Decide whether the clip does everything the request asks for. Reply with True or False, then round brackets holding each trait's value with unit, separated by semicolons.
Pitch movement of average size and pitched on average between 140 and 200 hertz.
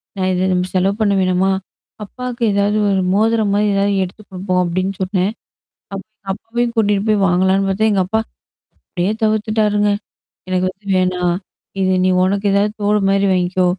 False (2.1 semitones; 195 Hz)